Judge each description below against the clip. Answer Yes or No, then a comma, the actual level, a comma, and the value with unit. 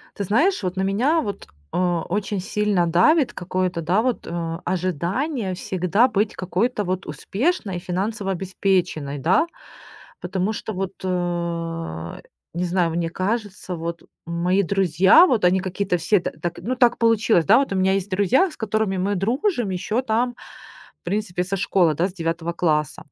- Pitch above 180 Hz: Yes, high, 190 Hz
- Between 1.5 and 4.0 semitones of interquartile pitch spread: Yes, average, 3.5 semitones